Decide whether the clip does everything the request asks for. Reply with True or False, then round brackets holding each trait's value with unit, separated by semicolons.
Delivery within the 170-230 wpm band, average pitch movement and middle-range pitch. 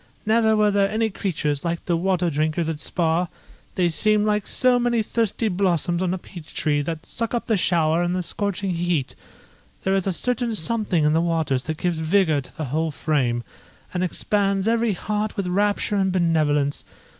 True (190 wpm; 4.5 semitones; 180 Hz)